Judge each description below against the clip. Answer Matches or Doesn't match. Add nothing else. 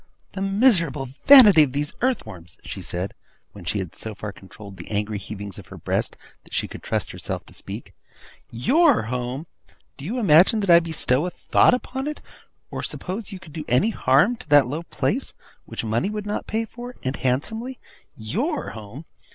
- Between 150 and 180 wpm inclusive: Doesn't match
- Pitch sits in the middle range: Matches